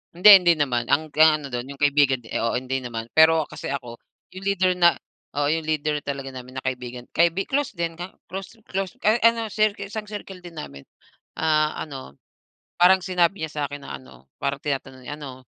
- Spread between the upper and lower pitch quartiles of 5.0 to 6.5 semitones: Yes, wide, 5.5 semitones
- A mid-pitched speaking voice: Yes, medium, 150 Hz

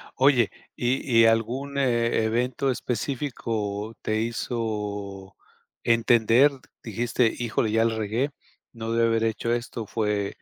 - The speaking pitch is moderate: No, low, 115 Hz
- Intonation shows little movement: Yes, narrow, 1.8 semitones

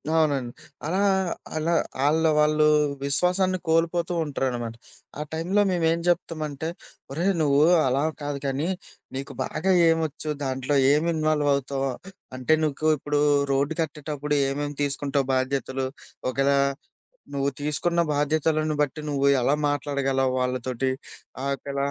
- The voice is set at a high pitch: No, medium, 145 Hz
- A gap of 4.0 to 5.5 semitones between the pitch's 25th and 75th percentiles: No, narrow, 2.5 semitones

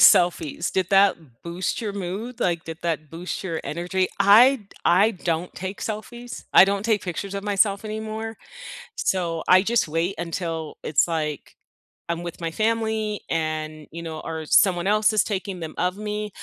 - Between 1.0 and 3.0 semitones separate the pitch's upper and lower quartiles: No, average, 4.1 semitones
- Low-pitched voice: No, medium, 185 Hz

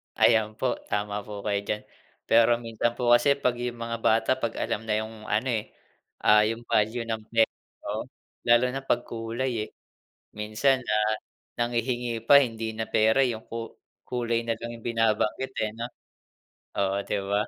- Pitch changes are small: Yes, narrow, 1.8 semitones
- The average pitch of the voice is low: Yes, low, 115 Hz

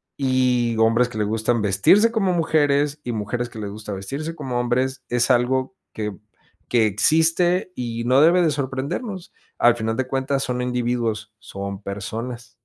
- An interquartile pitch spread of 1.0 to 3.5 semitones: No, average, 4.0 semitones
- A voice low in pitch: Yes, low, 125 Hz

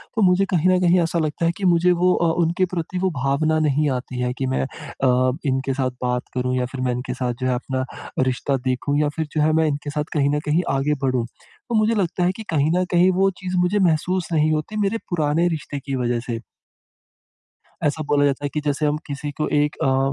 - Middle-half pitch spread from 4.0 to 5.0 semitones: Yes, average, 4.6 semitones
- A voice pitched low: No, medium, 150 Hz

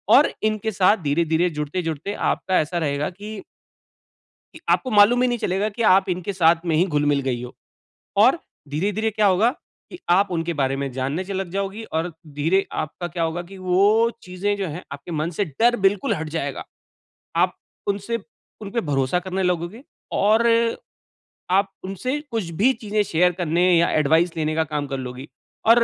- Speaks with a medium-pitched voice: Yes, medium, 180 Hz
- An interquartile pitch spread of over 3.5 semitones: Yes, average, 4.4 semitones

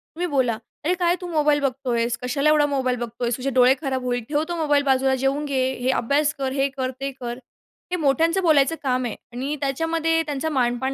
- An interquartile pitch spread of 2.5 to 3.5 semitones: Yes, average, 2.9 semitones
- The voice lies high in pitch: Yes, very high, 275 Hz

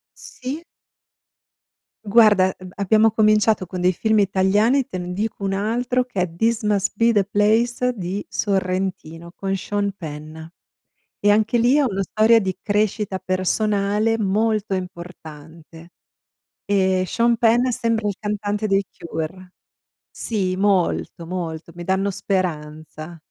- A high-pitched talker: Yes, high, 200 Hz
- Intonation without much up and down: No, average, 3.0 semitones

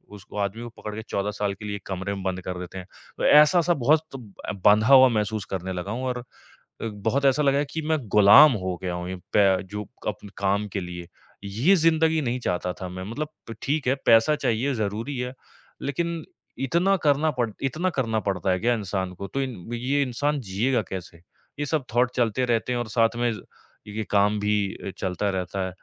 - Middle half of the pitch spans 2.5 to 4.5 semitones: No, wide, 5.5 semitones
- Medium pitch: No, low, 110 Hz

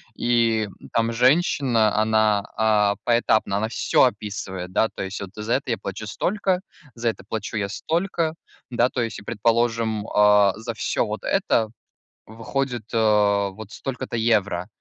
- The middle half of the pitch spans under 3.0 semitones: Yes, narrow, 2.4 semitones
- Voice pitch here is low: Yes, low, 110 Hz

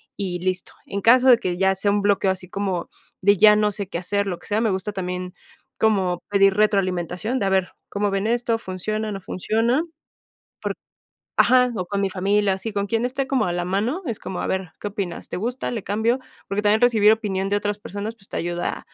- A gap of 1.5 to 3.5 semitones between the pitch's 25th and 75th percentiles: Yes, narrow, 2.6 semitones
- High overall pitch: Yes, high, 200 Hz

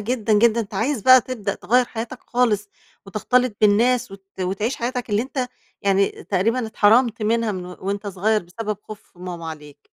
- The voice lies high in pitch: Yes, high, 215 Hz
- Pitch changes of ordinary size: Yes, average, 3.4 semitones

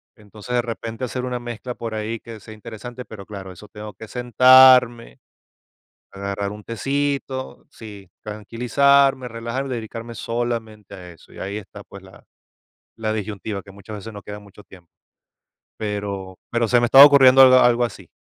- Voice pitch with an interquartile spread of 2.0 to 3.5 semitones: Yes, average, 3.1 semitones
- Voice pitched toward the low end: Yes, low, 115 Hz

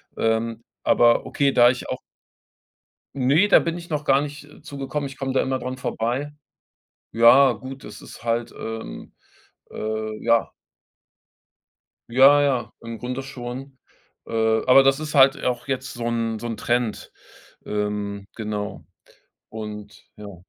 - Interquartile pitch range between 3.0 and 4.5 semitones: Yes, average, 3.3 semitones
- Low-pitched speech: Yes, low, 120 Hz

